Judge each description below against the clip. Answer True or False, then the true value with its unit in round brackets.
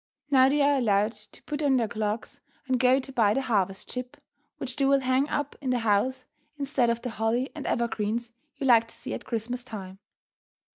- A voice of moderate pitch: False (245 Hz)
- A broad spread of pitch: False (3.2 semitones)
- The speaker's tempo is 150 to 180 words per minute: False (205 wpm)